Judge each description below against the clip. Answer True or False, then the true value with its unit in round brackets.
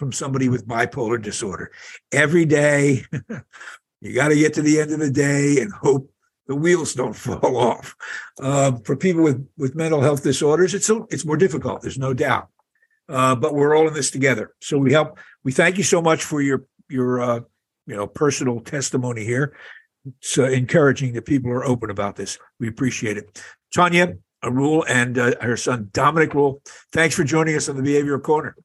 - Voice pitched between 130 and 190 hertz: True (140 Hz)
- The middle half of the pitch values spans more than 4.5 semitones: False (3.4 semitones)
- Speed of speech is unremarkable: True (190 wpm)